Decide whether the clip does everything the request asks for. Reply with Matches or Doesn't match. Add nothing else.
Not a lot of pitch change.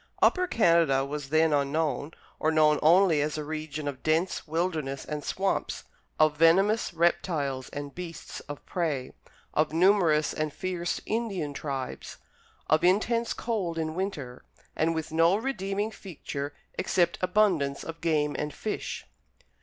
Doesn't match